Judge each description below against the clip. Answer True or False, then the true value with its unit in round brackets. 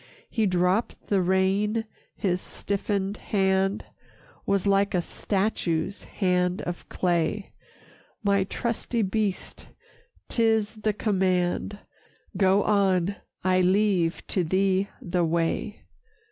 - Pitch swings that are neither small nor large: False (2.2 semitones)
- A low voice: False (195 Hz)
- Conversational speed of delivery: False (105 wpm)